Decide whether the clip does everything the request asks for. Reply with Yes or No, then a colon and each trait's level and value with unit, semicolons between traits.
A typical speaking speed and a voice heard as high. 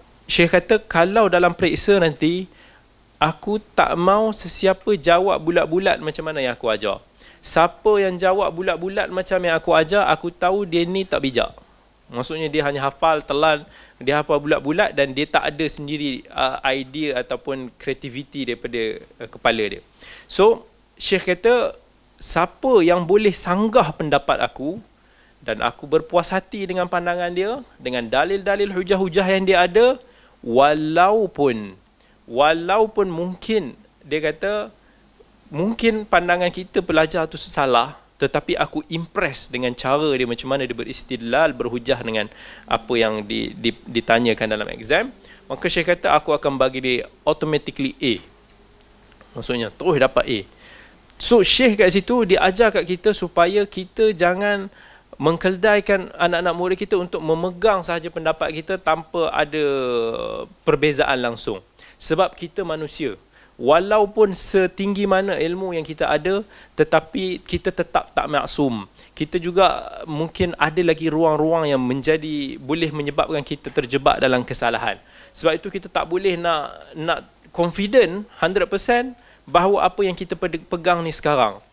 No: average, 135 wpm; medium, 170 Hz